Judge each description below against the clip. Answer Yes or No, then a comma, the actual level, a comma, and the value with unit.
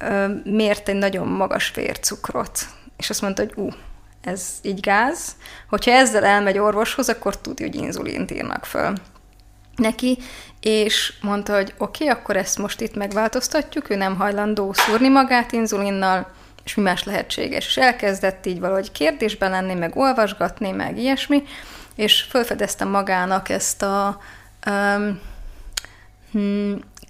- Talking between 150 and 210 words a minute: No, average, 135 wpm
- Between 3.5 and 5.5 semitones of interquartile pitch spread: No, narrow, 2.6 semitones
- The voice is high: Yes, high, 205 Hz